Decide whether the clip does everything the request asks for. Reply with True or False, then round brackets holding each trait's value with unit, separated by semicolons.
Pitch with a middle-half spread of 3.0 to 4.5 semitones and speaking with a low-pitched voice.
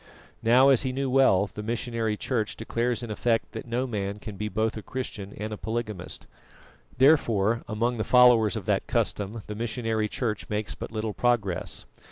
False (2.4 semitones; 115 Hz)